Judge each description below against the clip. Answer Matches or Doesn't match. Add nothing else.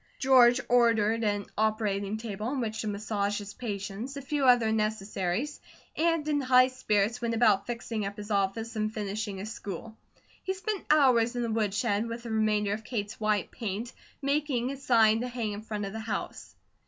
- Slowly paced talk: Doesn't match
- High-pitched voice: Matches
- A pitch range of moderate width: Matches